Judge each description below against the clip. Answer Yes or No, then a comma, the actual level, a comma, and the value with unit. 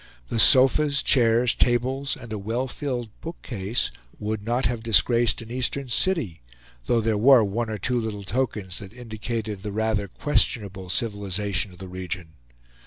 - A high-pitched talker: No, low, 110 Hz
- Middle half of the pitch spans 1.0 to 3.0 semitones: No, average, 3.4 semitones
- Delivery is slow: No, average, 155 wpm